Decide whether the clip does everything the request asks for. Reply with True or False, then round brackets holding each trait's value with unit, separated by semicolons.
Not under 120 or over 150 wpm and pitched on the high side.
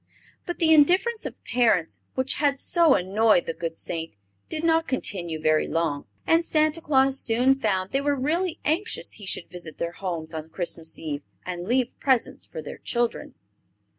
False (170 wpm; 240 Hz)